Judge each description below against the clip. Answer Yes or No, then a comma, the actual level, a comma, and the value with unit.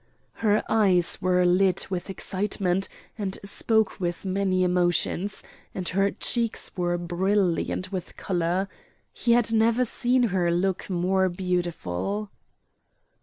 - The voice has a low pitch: No, high, 190 Hz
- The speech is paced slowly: Yes, slow, 120 wpm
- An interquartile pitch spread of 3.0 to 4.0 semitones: No, narrow, 2.4 semitones